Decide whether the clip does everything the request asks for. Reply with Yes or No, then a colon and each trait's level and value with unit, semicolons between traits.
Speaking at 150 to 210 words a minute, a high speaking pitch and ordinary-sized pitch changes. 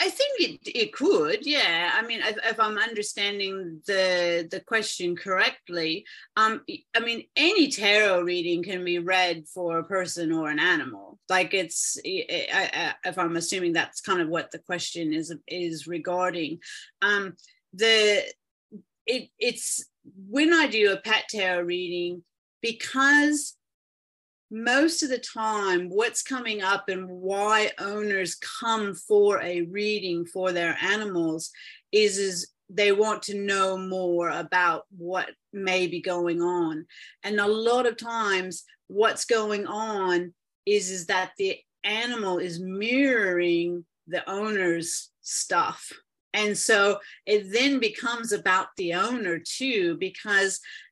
No: slow, 135 wpm; high, 200 Hz; average, 4.2 semitones